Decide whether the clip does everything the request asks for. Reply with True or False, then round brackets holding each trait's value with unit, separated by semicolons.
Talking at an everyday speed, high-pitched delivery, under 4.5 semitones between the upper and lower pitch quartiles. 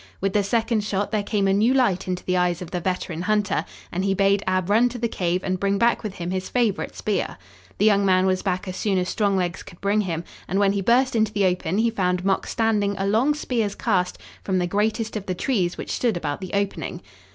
False (245 wpm; 195 Hz; 2.6 semitones)